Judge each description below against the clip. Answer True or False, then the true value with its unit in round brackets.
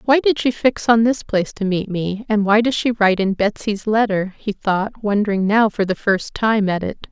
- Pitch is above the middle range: True (210 Hz)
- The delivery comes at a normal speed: False (235 wpm)